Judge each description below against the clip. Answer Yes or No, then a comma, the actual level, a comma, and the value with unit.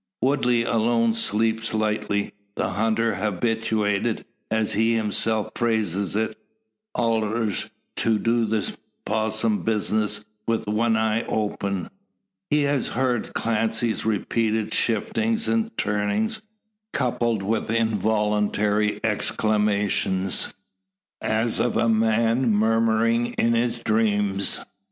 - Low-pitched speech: Yes, low, 110 Hz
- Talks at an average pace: No, slow, 100 wpm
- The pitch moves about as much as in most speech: No, narrow, 1.6 semitones